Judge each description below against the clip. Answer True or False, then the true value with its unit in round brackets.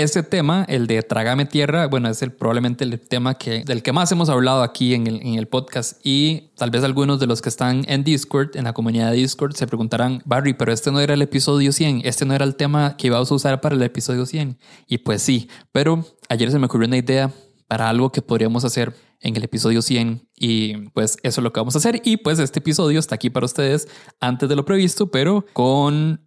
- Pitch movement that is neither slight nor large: True (3.2 semitones)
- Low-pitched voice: True (130 Hz)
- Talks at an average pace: False (240 wpm)